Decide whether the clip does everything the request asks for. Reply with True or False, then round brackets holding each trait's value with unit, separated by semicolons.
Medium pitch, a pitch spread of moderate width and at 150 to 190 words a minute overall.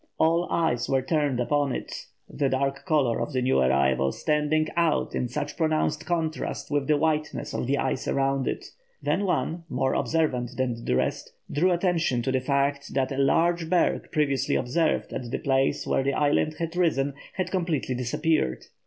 True (145 Hz; 3.5 semitones; 180 wpm)